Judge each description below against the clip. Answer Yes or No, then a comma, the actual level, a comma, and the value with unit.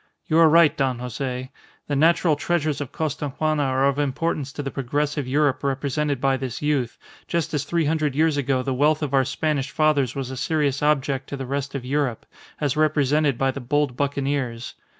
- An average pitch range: No, narrow, 2.2 semitones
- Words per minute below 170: No, average, 190 wpm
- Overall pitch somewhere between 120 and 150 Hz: Yes, medium, 140 Hz